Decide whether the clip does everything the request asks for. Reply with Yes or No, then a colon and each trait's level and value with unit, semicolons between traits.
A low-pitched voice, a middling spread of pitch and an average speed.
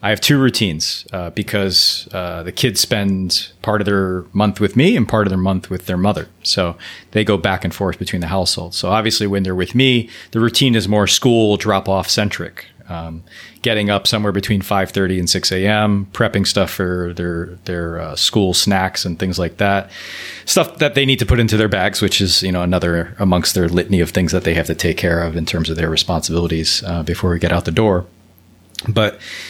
No: very low, 95 Hz; average, 3.2 semitones; fast, 220 wpm